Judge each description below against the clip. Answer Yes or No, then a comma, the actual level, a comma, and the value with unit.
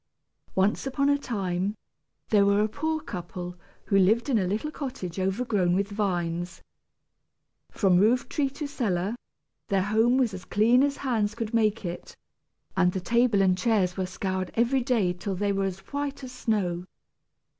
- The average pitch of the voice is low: No, high, 205 Hz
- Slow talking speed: No, average, 165 wpm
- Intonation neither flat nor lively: Yes, average, 4.6 semitones